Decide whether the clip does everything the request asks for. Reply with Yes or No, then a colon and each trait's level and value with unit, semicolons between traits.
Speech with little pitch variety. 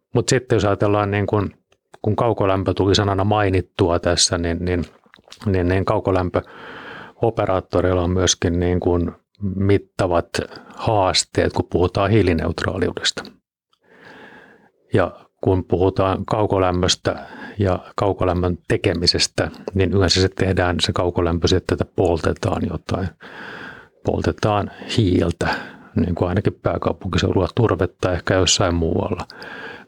Yes: narrow, 2.3 semitones